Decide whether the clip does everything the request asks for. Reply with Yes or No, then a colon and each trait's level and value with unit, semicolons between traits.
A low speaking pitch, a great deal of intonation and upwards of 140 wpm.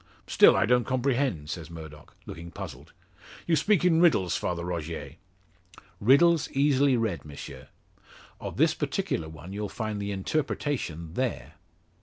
No: low, 105 Hz; wide, 8.7 semitones; slow, 135 wpm